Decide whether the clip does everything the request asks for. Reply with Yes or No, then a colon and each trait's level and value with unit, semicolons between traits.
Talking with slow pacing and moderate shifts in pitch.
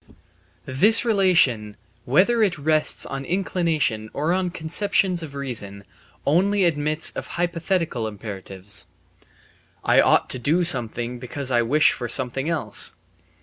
No: slow, 125 wpm; wide, 6.5 semitones